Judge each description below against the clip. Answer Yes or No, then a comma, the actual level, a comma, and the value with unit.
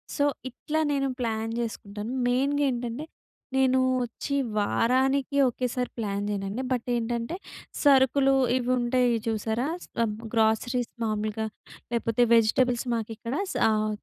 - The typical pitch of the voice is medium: No, high, 240 Hz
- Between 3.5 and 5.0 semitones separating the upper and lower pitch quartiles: No, average, 2.9 semitones